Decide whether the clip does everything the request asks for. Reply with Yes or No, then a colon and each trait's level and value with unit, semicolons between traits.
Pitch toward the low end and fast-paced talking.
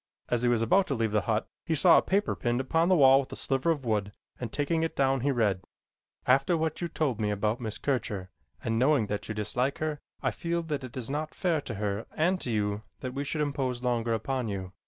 Yes: low, 130 Hz; fast, 240 wpm